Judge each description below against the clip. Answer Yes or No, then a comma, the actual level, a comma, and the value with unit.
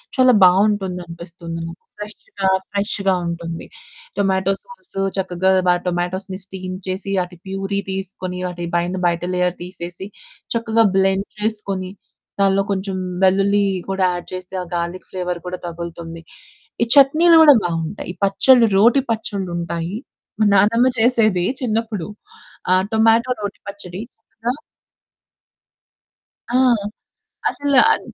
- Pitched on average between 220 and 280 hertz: No, high, 190 Hz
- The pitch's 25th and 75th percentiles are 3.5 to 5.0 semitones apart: No, average, 2.9 semitones